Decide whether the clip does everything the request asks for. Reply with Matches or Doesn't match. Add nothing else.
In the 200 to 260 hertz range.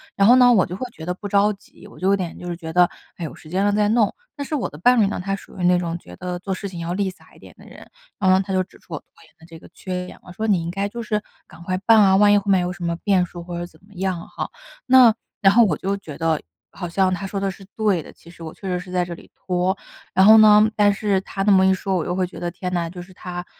Doesn't match